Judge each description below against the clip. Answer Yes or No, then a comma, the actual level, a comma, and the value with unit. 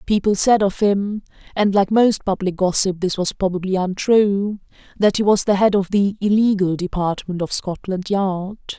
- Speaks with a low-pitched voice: No, high, 195 Hz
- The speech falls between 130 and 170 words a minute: Yes, average, 155 wpm